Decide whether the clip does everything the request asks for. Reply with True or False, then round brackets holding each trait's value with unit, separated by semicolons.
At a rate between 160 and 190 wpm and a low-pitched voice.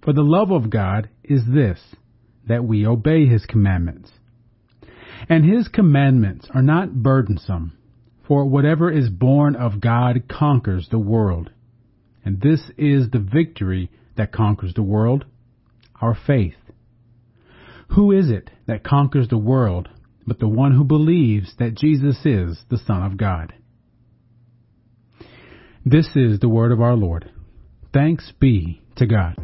False (140 wpm; 120 Hz)